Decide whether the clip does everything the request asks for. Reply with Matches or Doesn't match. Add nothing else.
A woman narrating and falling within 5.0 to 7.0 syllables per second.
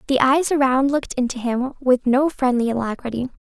Matches